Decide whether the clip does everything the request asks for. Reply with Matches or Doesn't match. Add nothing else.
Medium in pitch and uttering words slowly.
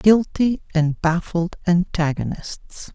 Matches